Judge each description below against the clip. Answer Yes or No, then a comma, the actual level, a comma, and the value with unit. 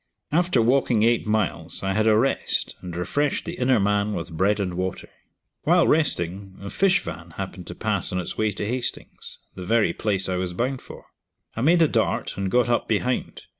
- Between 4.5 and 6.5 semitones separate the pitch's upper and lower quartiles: Yes, average, 5.2 semitones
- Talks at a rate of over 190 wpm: Yes, average, 200 wpm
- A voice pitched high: No, low, 110 Hz